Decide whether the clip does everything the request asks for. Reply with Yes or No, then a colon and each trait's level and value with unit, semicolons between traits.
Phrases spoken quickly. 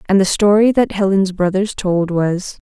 No: average, 180 wpm